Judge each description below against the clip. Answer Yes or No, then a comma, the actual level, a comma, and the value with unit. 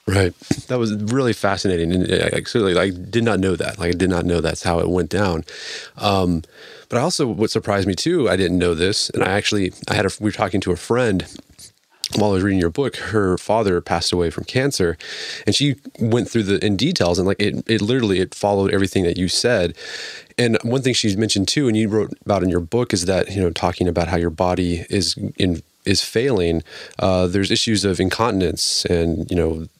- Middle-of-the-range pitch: No, very low, 95 Hz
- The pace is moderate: No, fast, 225 wpm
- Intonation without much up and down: No, average, 3.3 semitones